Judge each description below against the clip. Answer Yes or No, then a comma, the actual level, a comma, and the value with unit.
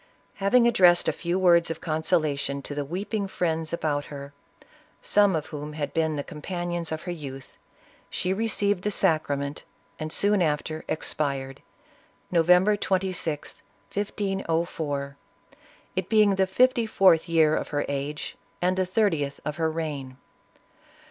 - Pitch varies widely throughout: No, average, 4.3 semitones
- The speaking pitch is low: No, medium, 165 Hz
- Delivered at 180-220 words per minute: No, average, 140 wpm